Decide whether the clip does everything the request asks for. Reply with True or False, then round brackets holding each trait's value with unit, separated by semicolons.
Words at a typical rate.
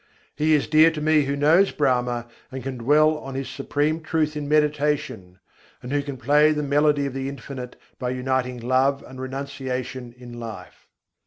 True (175 wpm)